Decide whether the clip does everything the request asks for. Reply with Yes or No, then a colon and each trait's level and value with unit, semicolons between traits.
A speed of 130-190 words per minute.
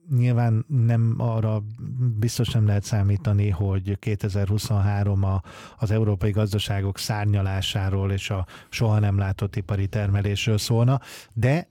No: average, 120 wpm